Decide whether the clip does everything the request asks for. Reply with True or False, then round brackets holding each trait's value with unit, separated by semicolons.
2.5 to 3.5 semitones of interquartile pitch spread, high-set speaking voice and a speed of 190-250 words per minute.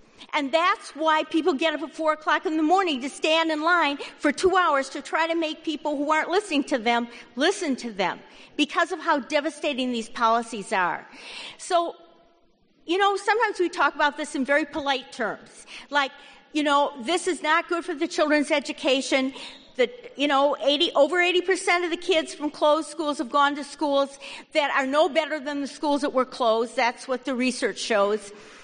True (3.0 semitones; 300 Hz; 195 wpm)